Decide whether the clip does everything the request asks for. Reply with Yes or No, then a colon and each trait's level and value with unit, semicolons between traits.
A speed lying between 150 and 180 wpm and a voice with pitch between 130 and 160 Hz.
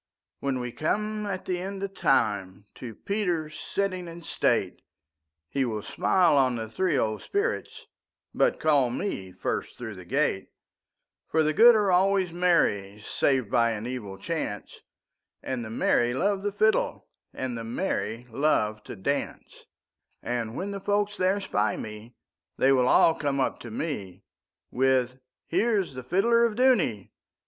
No: average, 140 wpm; low, 135 Hz